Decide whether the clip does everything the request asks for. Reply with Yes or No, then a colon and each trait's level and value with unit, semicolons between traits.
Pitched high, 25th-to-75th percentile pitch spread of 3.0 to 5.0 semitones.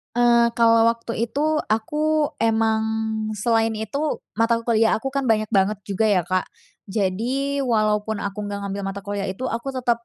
No: high, 225 Hz; narrow, 2.6 semitones